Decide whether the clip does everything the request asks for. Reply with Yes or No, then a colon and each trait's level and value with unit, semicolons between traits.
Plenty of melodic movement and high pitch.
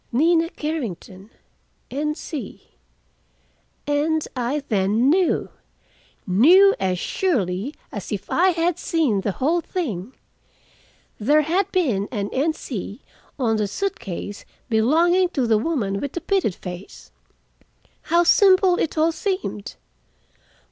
Yes: wide, 8.4 semitones; very high, 290 Hz